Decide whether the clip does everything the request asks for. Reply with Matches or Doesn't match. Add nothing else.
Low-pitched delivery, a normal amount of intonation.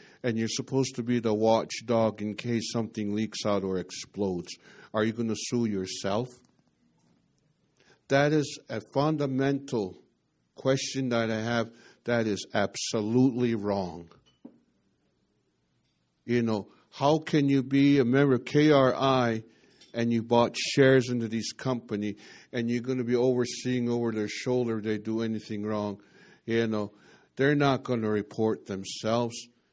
Matches